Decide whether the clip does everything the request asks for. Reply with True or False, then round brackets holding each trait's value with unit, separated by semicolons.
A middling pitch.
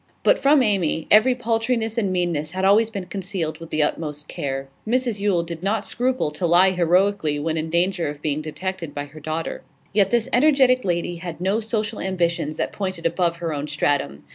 True (180 Hz)